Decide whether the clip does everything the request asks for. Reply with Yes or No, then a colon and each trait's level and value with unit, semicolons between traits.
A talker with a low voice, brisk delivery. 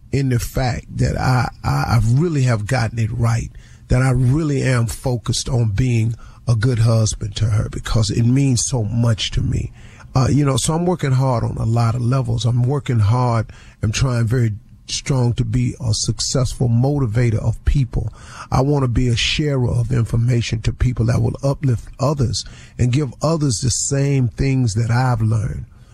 No: low, 120 Hz; average, 185 wpm